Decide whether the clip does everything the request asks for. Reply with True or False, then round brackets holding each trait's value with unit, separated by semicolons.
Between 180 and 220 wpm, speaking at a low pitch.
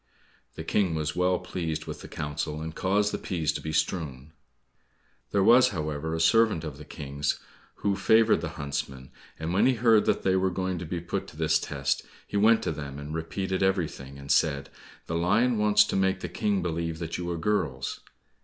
True (200 wpm; 85 Hz)